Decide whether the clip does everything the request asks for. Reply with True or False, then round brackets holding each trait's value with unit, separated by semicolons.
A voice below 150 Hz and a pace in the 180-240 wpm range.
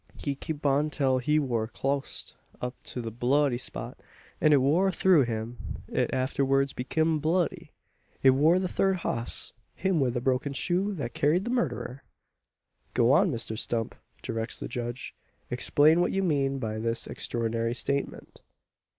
False (135 Hz; 160 wpm)